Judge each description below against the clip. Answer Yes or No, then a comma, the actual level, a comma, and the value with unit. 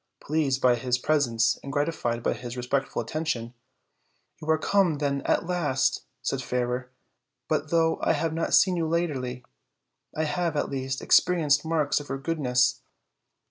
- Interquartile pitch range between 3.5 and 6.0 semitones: Yes, average, 4.1 semitones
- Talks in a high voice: No, medium, 140 Hz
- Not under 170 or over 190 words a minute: No, average, 160 wpm